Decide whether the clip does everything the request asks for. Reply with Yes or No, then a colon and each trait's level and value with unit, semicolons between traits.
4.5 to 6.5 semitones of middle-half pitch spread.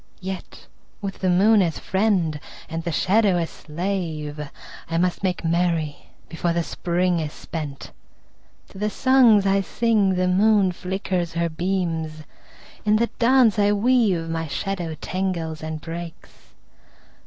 No: average, 3.4 semitones